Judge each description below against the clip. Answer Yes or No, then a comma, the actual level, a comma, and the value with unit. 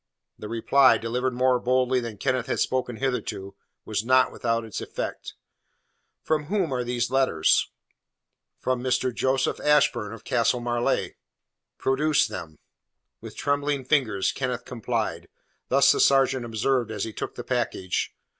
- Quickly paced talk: No, average, 140 wpm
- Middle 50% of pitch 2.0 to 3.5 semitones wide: Yes, narrow, 2.6 semitones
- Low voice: Yes, low, 125 Hz